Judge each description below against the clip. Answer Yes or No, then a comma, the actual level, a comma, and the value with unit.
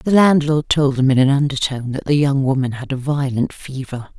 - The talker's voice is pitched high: No, medium, 140 Hz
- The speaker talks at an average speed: No, fast, 215 wpm